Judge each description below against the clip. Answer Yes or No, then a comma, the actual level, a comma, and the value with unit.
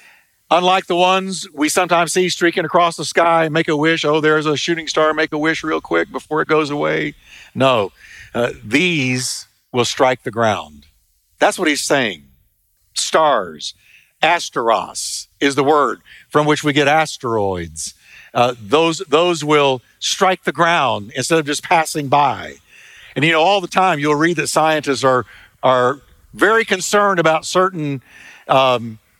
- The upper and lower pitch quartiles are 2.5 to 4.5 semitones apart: No, average, 4.9 semitones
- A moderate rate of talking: Yes, average, 160 wpm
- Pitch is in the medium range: Yes, medium, 155 Hz